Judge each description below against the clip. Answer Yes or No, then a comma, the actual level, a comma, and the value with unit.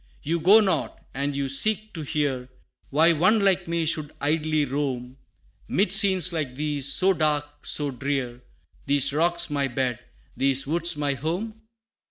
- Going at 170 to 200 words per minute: No, average, 155 wpm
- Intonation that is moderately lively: Yes, average, 3.8 semitones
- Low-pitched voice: No, medium, 150 Hz